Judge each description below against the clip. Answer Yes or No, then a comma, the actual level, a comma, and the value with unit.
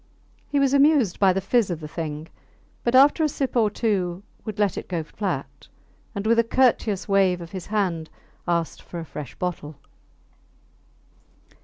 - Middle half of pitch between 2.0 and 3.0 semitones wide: No, average, 5.2 semitones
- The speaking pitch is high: Yes, high, 195 Hz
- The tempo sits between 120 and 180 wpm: Yes, average, 170 wpm